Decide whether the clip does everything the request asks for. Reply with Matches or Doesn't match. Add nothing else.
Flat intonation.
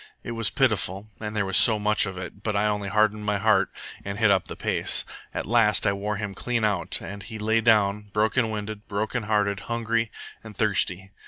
Matches